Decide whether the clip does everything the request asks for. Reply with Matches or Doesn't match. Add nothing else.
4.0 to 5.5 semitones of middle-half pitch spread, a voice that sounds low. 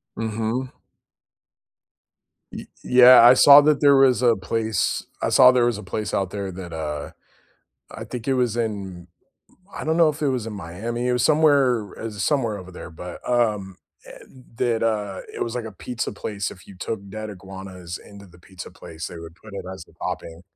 Matches